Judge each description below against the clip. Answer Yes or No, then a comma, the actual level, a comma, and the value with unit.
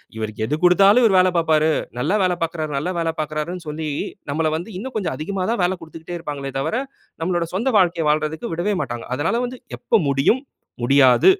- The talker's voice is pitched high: No, medium, 165 Hz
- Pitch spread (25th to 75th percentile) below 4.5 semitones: Yes, average, 3.8 semitones